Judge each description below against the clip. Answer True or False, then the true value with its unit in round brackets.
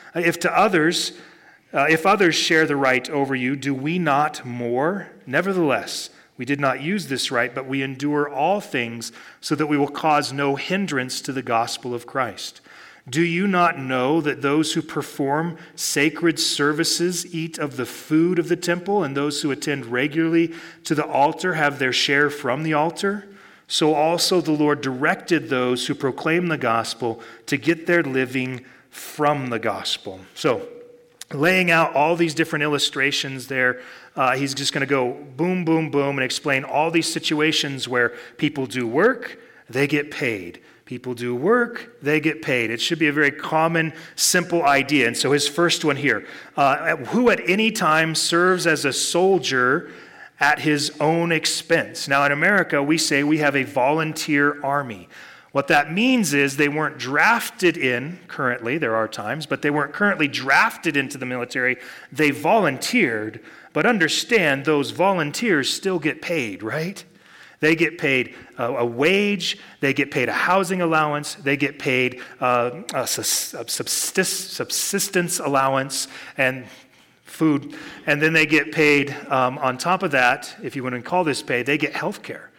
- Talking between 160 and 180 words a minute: True (165 wpm)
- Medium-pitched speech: True (150 Hz)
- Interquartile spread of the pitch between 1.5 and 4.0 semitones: True (3.7 semitones)